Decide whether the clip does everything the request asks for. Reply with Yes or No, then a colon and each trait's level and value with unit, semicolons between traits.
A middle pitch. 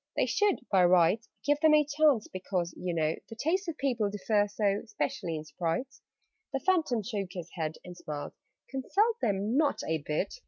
No: high, 210 Hz